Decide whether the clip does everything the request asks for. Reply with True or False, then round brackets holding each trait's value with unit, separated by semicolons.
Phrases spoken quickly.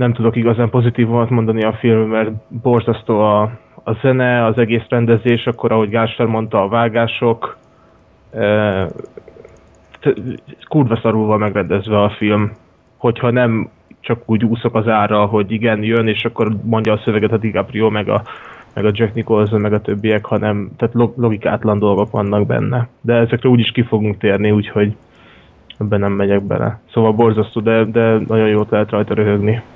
True (160 wpm)